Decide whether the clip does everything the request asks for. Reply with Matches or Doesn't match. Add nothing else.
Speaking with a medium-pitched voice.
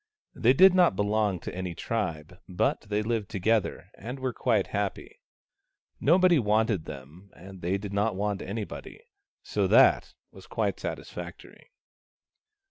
Doesn't match